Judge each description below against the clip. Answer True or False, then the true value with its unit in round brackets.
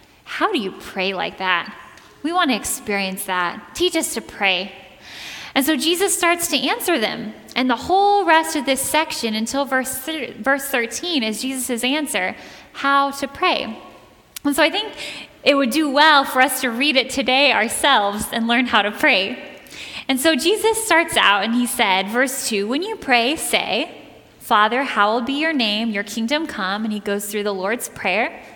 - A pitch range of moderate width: False (5.9 semitones)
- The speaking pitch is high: True (265 Hz)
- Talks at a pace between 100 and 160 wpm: False (190 wpm)